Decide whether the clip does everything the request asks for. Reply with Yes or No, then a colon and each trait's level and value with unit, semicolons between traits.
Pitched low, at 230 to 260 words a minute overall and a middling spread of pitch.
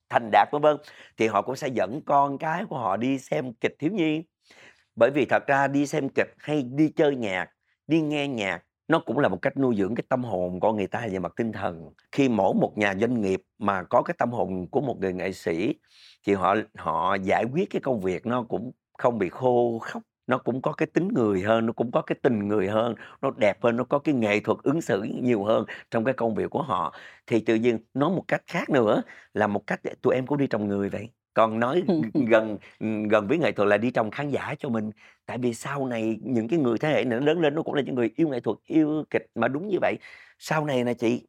Yes: low, 115 Hz; fast, 250 wpm; average, 4.9 semitones